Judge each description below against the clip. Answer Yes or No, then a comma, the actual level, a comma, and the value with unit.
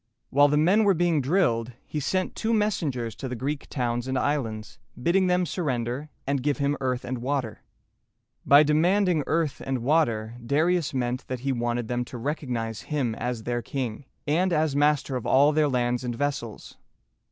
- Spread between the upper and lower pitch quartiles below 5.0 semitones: Yes, average, 4.1 semitones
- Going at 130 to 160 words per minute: No, average, 175 wpm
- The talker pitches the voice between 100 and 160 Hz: Yes, medium, 140 Hz